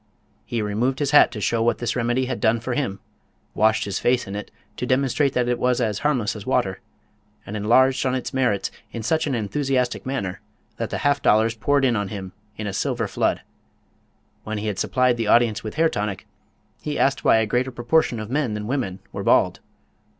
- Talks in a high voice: No, low, 120 Hz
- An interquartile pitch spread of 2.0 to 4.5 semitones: Yes, average, 3.5 semitones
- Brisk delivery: Yes, fast, 210 wpm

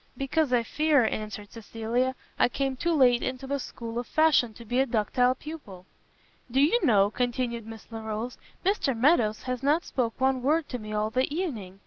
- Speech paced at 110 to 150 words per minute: No, average, 185 wpm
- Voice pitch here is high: Yes, very high, 250 Hz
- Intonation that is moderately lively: Yes, average, 3.7 semitones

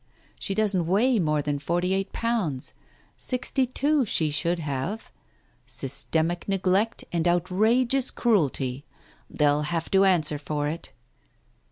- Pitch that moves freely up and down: Yes, wide, 6.1 semitones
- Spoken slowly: Yes, slow, 125 wpm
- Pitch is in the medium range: Yes, medium, 175 Hz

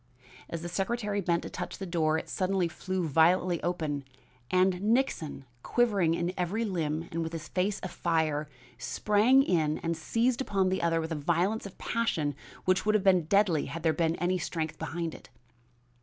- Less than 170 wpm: No, average, 180 wpm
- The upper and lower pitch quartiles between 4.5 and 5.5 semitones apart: No, average, 3.4 semitones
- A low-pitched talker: No, medium, 175 Hz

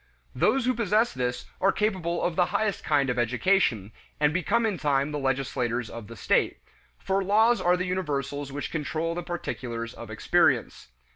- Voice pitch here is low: No, medium, 160 Hz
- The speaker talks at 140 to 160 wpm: No, average, 170 wpm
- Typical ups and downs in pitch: No, wide, 6.7 semitones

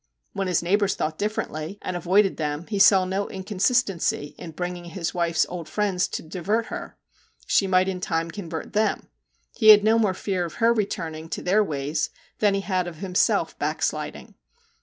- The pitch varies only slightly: No, average, 3.3 semitones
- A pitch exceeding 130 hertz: Yes, medium, 185 Hz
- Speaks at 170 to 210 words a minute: Yes, average, 180 wpm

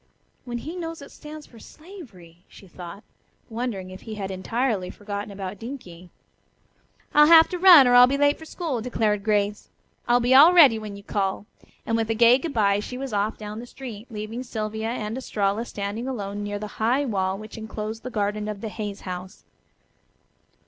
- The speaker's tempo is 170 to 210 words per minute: Yes, average, 190 wpm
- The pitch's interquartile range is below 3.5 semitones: No, average, 3.8 semitones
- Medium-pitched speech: No, high, 220 Hz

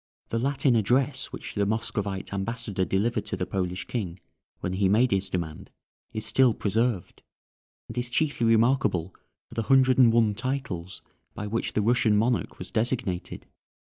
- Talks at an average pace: Yes, average, 160 wpm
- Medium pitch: No, low, 110 Hz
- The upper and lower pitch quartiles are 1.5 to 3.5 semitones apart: No, average, 4.0 semitones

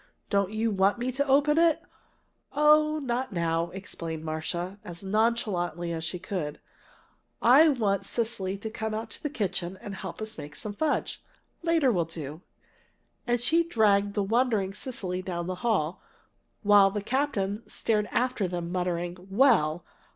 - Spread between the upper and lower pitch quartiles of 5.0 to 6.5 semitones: Yes, average, 5.3 semitones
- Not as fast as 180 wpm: Yes, average, 155 wpm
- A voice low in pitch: No, high, 200 Hz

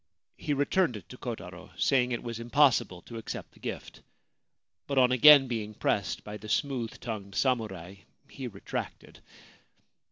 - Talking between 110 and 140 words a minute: No, average, 155 wpm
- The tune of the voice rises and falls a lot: No, average, 4.0 semitones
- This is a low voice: Yes, low, 120 Hz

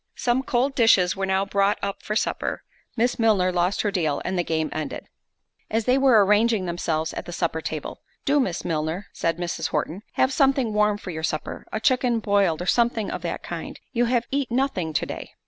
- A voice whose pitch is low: No, high, 200 Hz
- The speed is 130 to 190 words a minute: No, average, 200 wpm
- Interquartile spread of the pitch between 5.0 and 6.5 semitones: Yes, wide, 5.5 semitones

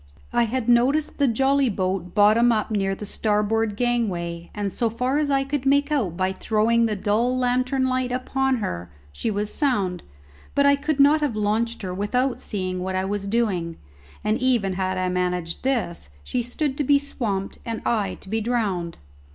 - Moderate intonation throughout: Yes, average, 4.8 semitones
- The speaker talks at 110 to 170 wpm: No, average, 185 wpm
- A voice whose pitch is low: No, high, 225 Hz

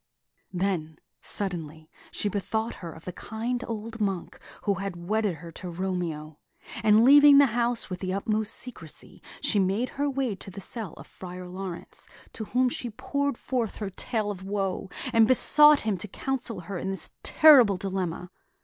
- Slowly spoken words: No, average, 170 wpm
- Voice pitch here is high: Yes, high, 200 Hz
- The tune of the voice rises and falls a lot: No, average, 4.3 semitones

